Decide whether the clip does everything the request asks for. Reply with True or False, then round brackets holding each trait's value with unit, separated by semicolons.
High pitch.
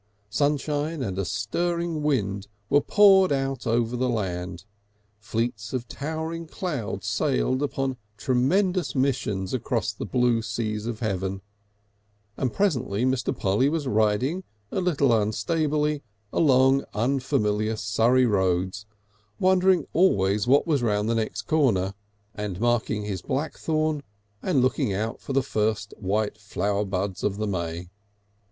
False (120 Hz)